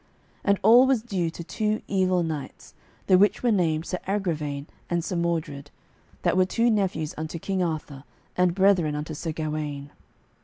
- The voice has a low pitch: No, medium, 170 Hz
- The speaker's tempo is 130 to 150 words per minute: No, average, 160 wpm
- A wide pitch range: No, average, 3.9 semitones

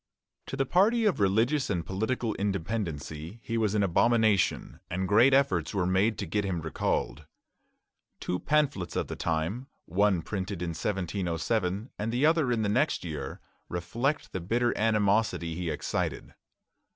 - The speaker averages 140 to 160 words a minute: Yes, average, 150 wpm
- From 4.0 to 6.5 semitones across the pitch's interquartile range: Yes, average, 4.9 semitones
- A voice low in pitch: Yes, low, 105 Hz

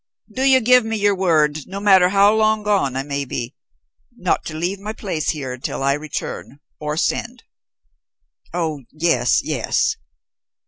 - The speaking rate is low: No, average, 155 wpm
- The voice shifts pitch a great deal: Yes, wide, 6.0 semitones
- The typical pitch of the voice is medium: Yes, medium, 175 Hz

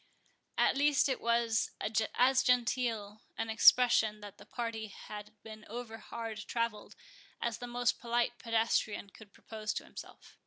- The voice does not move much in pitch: Yes, narrow, 1.9 semitones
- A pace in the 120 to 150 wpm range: Yes, average, 140 wpm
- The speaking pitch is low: No, high, 230 Hz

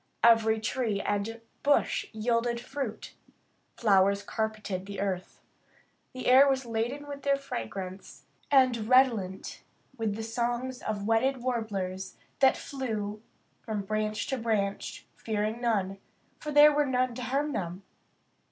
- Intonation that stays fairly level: No, average, 4.0 semitones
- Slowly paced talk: Yes, slow, 130 wpm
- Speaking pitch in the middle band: No, high, 225 Hz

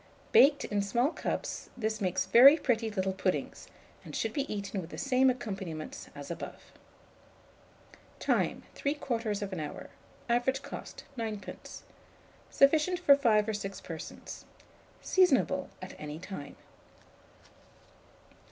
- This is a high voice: Yes, high, 220 Hz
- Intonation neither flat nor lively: No, wide, 5.9 semitones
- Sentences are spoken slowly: Yes, slow, 115 wpm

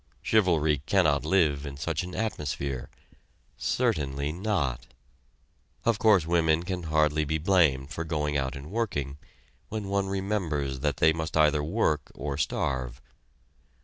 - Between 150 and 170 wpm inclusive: No, slow, 135 wpm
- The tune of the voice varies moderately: Yes, average, 4.5 semitones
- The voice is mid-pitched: No, very low, 80 Hz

